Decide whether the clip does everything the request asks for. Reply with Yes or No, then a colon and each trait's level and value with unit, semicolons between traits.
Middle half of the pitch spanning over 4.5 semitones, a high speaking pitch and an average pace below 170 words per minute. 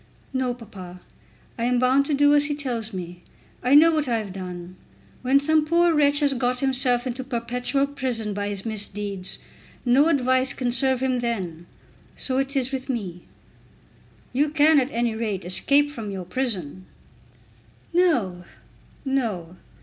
Yes: average, 5.3 semitones; very high, 250 Hz; average, 155 wpm